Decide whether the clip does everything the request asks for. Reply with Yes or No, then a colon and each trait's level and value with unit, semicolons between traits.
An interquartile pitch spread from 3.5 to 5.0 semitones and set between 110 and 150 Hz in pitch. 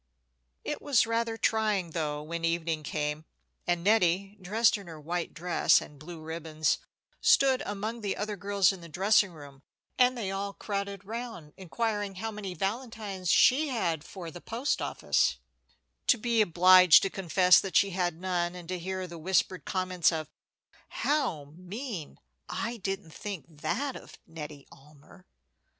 No: average, 4.2 semitones; medium, 185 Hz